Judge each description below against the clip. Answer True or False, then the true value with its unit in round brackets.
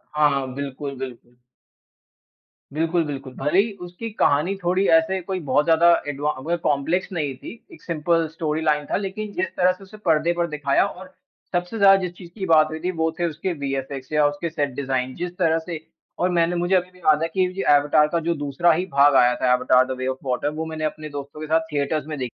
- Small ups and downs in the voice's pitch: False (3.7 semitones)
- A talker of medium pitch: True (155 Hz)